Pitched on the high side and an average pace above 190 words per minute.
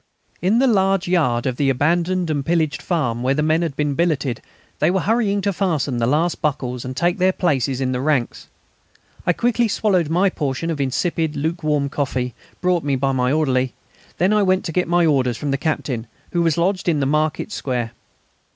No: medium, 155 Hz; average, 200 wpm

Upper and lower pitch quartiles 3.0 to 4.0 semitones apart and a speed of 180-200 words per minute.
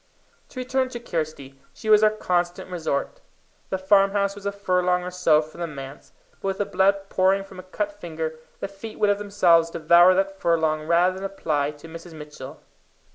Yes: average, 3.6 semitones; average, 190 wpm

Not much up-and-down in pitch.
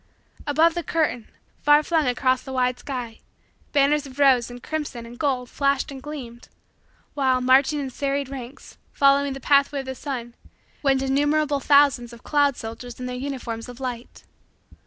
Yes: narrow, 2.3 semitones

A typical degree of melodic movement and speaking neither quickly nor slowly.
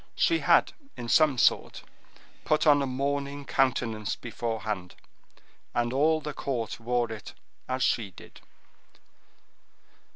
No: average, 3.7 semitones; slow, 120 wpm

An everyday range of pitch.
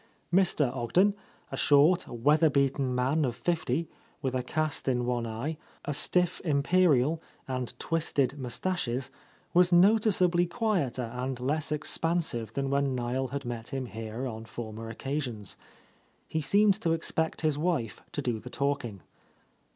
Yes: average, 4.9 semitones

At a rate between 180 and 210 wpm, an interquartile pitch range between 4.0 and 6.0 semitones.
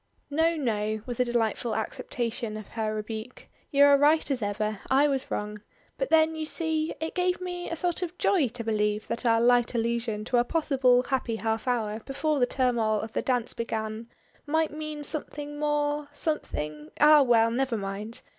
Yes: average, 185 wpm; average, 5.2 semitones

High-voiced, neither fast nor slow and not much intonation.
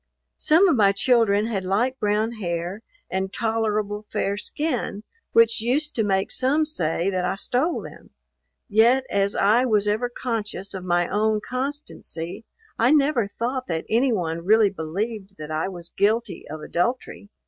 No: high, 210 Hz; average, 160 wpm; average, 4.0 semitones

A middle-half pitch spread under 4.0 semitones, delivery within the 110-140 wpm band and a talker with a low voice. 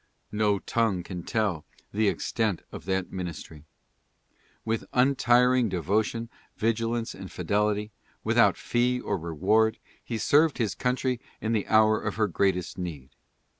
Yes: average, 3.5 semitones; slow, 135 wpm; low, 110 Hz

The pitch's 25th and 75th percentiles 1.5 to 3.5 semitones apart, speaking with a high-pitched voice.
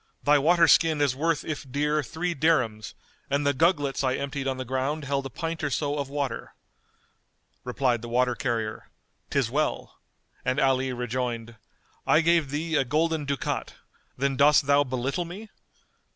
No: average, 3.1 semitones; medium, 140 Hz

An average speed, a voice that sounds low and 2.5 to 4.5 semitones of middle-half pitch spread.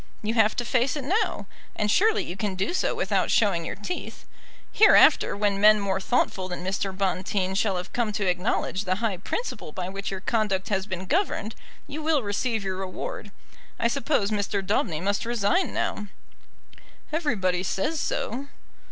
No: average, 170 wpm; high, 205 Hz; average, 3.9 semitones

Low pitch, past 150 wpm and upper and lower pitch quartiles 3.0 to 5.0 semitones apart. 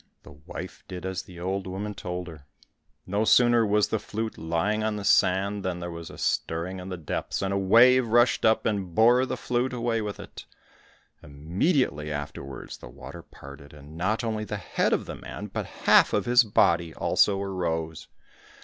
Yes: very low, 95 Hz; average, 185 wpm; average, 4.6 semitones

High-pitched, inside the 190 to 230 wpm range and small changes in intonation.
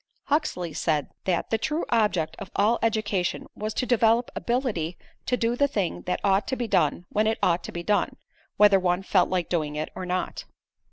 No: high, 200 Hz; average, 200 wpm; average, 4.5 semitones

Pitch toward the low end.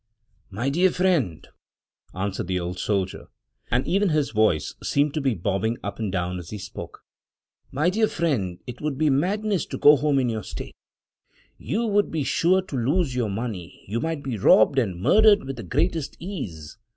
Yes: low, 130 Hz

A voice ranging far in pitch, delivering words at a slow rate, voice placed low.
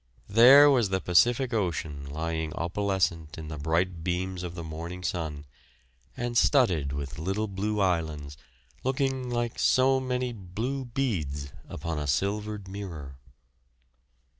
Yes: wide, 6.6 semitones; slow, 130 wpm; very low, 95 Hz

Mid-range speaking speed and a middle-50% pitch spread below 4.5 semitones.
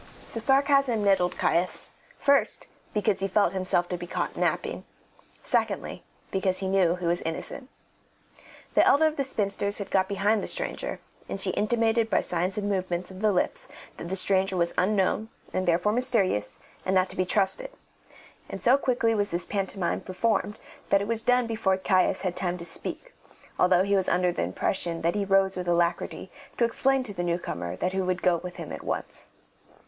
Yes: average, 190 wpm; average, 3.6 semitones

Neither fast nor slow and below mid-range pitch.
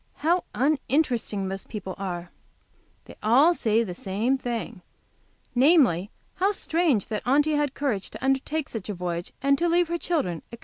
No: average, 165 wpm; high, 245 Hz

